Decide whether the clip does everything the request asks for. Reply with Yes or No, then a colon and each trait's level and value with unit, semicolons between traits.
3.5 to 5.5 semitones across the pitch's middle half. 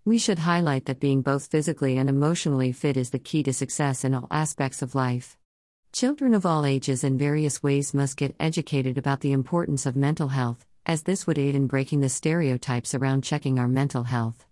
No: narrow, 2.5 semitones